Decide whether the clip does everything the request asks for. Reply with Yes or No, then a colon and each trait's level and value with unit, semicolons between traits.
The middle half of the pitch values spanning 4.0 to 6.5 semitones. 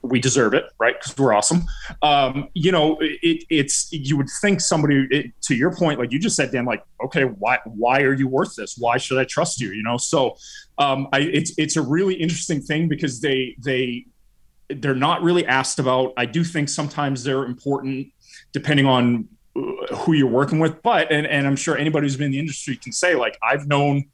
No: average, 3.3 semitones